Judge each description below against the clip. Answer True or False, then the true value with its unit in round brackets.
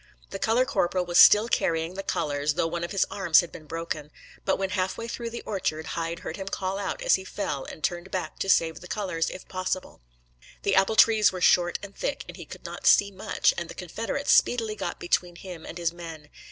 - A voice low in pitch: False (185 Hz)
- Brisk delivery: True (230 wpm)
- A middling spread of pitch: True (3.2 semitones)